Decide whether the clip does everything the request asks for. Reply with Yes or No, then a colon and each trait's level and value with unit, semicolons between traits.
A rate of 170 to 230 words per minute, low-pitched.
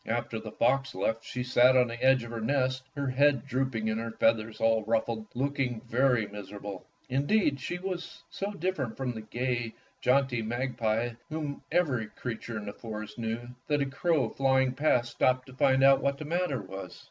Yes: average, 190 wpm; low, 125 Hz